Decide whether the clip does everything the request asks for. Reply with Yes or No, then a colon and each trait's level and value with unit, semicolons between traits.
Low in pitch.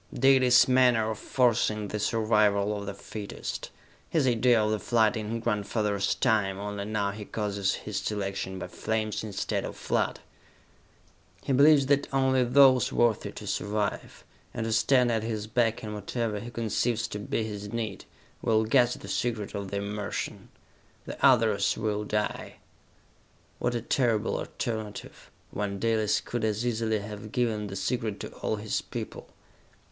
Yes: low, 110 Hz